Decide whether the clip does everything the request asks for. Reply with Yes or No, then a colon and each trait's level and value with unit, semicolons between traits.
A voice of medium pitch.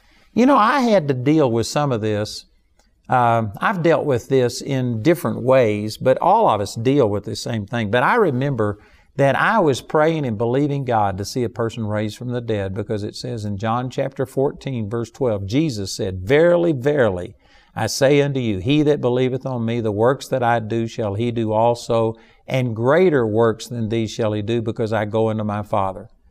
No: low, 115 Hz